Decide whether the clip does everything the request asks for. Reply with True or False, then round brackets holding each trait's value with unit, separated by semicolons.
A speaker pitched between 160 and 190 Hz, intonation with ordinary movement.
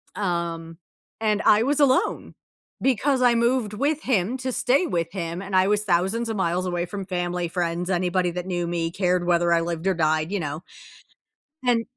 True (185 Hz; 4.6 semitones)